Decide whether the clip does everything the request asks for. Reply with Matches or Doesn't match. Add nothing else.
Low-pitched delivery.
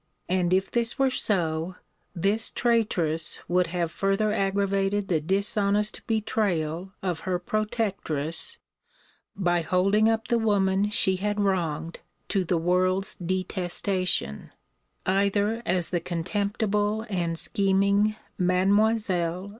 Doesn't match